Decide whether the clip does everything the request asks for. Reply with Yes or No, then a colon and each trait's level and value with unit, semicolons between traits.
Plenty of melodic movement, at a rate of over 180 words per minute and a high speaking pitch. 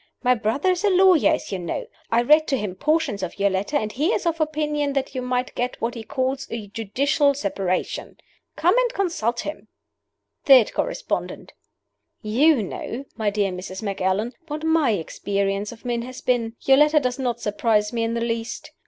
Yes: wide, 6.0 semitones; average, 190 wpm; high, 245 Hz